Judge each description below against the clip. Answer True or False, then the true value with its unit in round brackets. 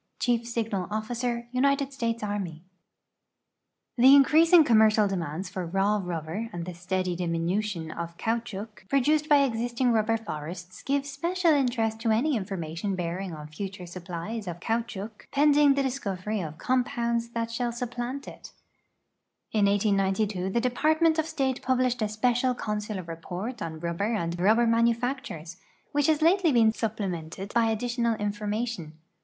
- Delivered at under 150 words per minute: True (140 wpm)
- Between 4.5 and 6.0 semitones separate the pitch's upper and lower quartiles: True (4.9 semitones)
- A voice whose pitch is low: False (220 Hz)